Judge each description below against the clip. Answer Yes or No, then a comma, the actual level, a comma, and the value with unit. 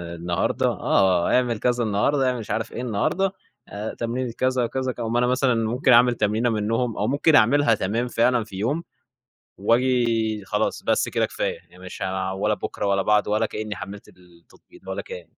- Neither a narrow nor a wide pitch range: Yes, average, 3.4 semitones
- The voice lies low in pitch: Yes, low, 115 Hz